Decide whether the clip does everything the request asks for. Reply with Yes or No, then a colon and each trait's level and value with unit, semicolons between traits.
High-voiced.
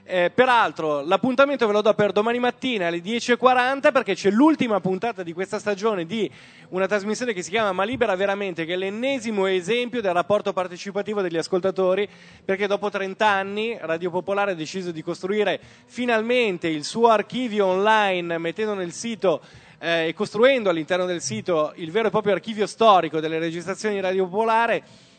Yes: high, 200 Hz